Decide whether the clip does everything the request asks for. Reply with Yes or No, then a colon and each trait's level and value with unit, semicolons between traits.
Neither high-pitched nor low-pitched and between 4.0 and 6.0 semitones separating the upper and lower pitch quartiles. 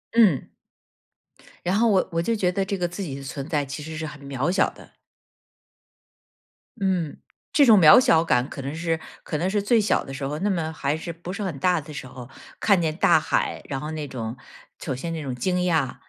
Yes: medium, 160 Hz; average, 4.7 semitones